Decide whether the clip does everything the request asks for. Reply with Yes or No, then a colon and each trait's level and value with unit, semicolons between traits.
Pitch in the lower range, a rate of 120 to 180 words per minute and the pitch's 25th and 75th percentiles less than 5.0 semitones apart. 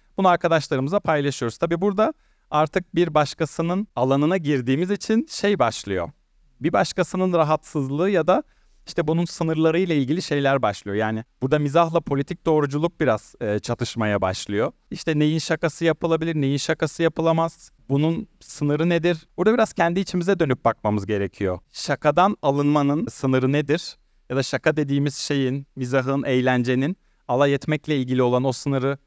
No: medium, 150 Hz; fast, 140 wpm; average, 4.0 semitones